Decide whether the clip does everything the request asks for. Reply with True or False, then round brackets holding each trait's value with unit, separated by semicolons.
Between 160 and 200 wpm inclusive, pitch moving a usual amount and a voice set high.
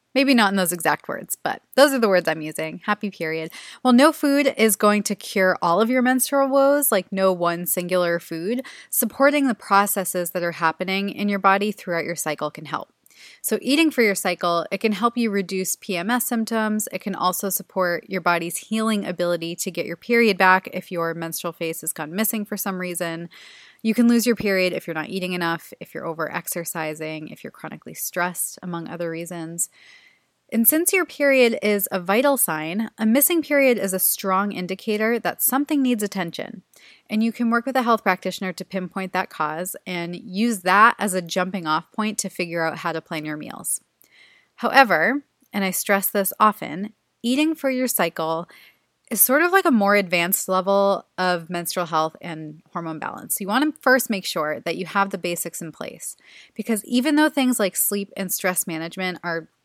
True (195 wpm; 5.0 semitones; 195 Hz)